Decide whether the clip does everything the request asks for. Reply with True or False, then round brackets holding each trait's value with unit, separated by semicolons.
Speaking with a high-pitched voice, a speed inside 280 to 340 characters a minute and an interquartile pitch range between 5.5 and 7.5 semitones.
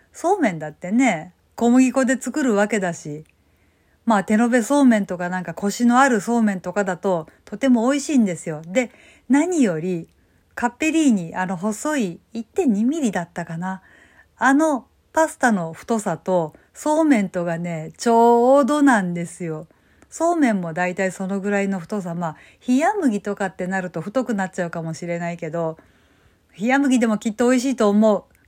True (210 Hz; 335 characters per minute; 6.2 semitones)